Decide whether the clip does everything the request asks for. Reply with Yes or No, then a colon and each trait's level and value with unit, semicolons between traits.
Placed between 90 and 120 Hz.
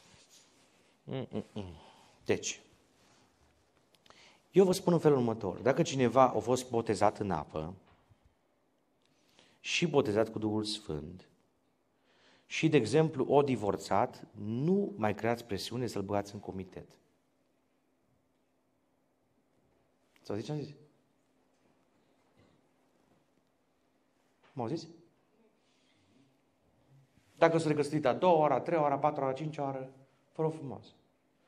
No: low, 130 Hz